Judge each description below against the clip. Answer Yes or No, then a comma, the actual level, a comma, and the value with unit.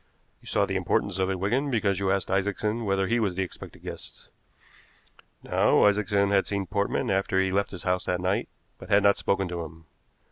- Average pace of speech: No, fast, 210 wpm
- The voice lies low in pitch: Yes, low, 100 Hz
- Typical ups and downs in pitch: No, narrow, 1.4 semitones